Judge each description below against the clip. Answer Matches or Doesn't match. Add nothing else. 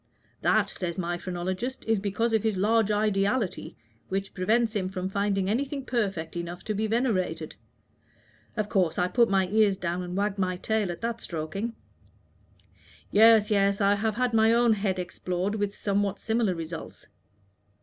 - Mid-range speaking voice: Doesn't match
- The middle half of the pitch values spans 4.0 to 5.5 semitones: Doesn't match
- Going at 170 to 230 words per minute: Doesn't match